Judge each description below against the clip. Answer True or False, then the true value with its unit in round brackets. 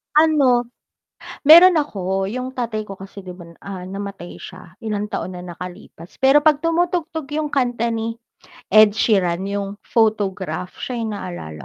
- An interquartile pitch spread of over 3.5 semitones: True (5.6 semitones)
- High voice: True (215 Hz)